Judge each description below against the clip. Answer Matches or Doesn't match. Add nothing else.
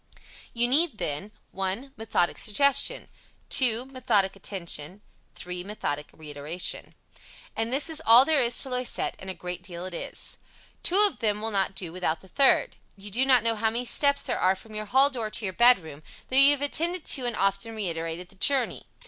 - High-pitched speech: Matches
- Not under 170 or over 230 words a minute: Matches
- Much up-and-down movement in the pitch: Matches